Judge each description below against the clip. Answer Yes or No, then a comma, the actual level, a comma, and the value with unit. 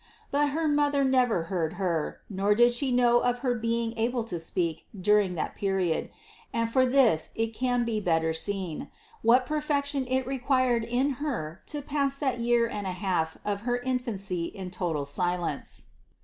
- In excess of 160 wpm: Yes, average, 175 wpm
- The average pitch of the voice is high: Yes, high, 230 Hz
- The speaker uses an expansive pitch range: Yes, wide, 5.8 semitones